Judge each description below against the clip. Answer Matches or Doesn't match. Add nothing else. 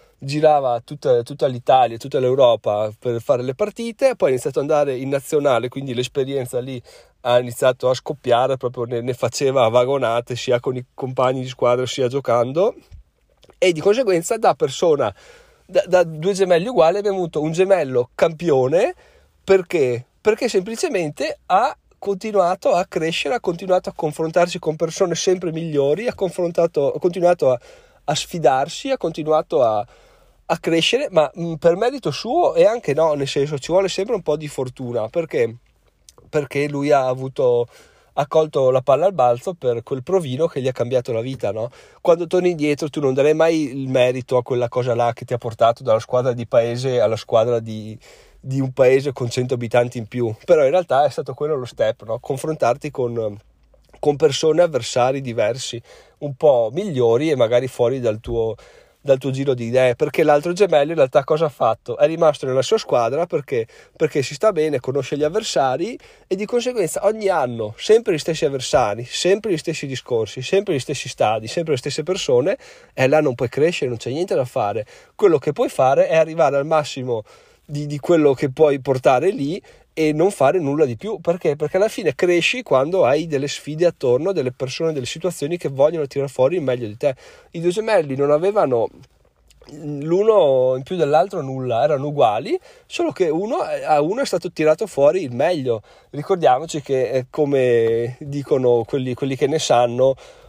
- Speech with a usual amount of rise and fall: Doesn't match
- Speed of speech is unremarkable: Doesn't match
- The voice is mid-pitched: Matches